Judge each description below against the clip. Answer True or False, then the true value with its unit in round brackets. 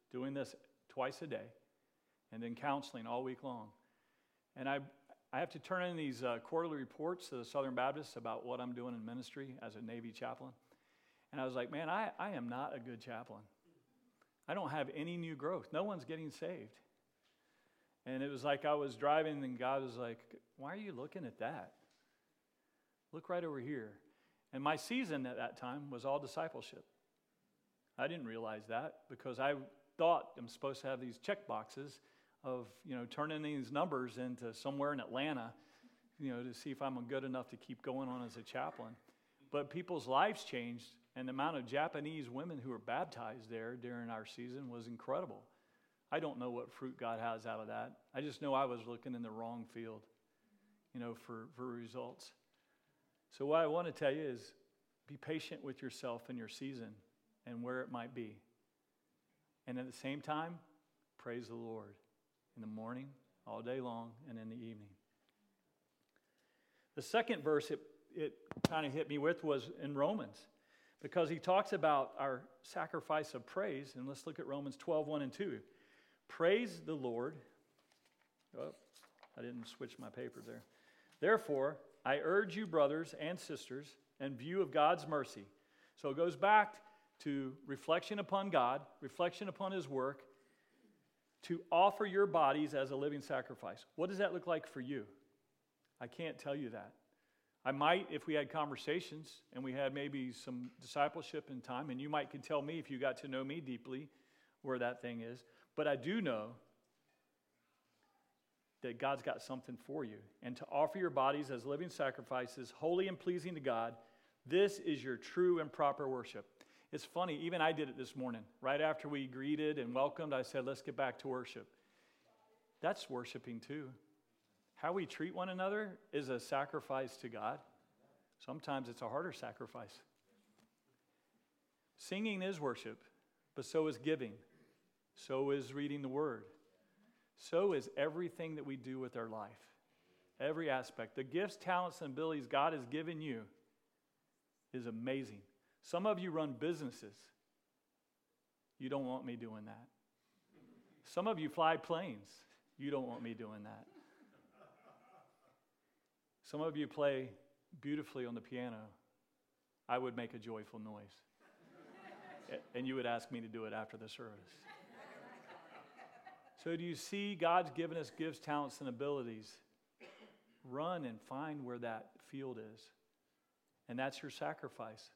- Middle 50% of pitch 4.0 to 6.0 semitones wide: True (4.4 semitones)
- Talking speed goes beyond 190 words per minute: False (170 wpm)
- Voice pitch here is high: False (135 Hz)